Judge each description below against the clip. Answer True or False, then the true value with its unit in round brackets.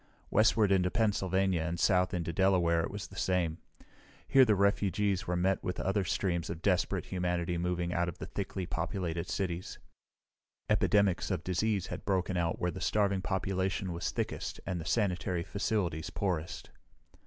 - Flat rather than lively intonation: True (2.1 semitones)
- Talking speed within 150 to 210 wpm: True (160 wpm)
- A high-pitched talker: False (90 Hz)